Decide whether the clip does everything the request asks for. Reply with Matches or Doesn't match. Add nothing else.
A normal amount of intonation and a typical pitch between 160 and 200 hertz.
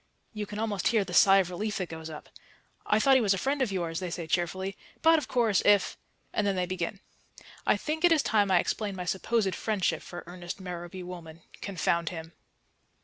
Matches